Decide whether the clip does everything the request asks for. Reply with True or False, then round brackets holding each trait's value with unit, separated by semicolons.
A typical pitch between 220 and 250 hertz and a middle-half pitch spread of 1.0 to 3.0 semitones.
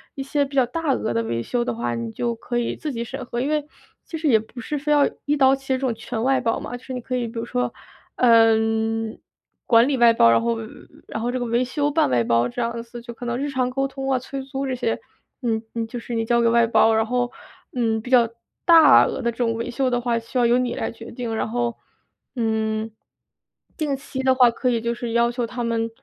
True (240 Hz; 2.4 semitones)